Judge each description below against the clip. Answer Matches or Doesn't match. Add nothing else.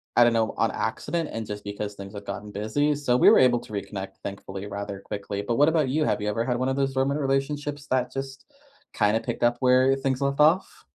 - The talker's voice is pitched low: Matches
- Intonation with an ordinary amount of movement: Matches